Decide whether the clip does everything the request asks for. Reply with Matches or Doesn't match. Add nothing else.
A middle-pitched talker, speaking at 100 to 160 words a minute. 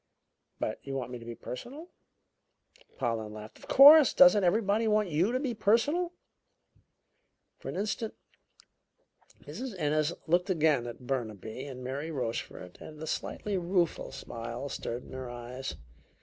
Matches